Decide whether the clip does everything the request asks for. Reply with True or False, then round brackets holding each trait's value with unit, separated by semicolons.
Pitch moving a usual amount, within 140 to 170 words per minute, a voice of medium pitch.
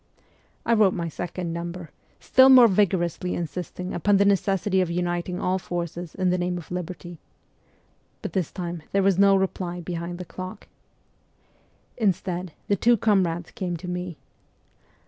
False (1.9 semitones; 150 wpm; 180 Hz)